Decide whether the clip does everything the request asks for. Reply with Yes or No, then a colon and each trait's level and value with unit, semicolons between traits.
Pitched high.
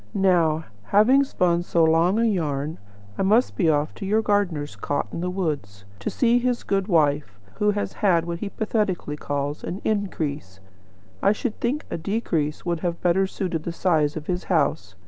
No: medium, 175 Hz